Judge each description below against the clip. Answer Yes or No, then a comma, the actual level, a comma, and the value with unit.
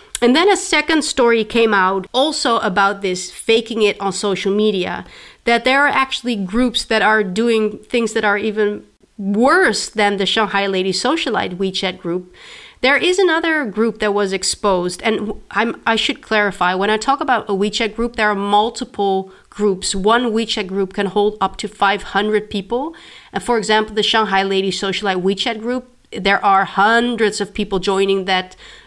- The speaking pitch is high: Yes, high, 210 Hz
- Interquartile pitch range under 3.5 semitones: Yes, average, 3.1 semitones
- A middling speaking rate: Yes, average, 175 wpm